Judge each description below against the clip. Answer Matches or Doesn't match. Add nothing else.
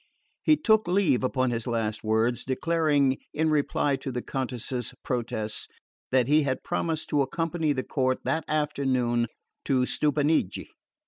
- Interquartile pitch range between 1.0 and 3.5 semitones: Doesn't match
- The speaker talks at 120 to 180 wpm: Matches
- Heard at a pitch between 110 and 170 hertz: Matches